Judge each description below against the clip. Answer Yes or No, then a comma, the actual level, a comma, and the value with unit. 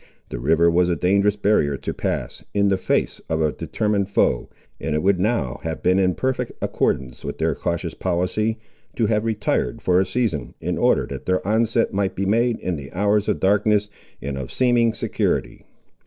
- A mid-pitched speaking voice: No, very low, 95 Hz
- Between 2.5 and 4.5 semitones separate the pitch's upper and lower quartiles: Yes, average, 4.1 semitones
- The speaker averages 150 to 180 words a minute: No, average, 190 wpm